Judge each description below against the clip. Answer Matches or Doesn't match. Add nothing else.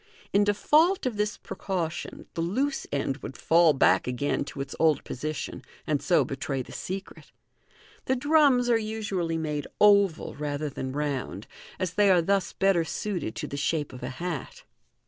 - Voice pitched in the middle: Matches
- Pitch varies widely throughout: Matches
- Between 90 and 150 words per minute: Doesn't match